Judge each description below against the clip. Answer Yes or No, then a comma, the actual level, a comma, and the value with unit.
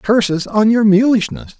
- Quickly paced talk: No, average, 150 wpm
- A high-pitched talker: Yes, high, 210 Hz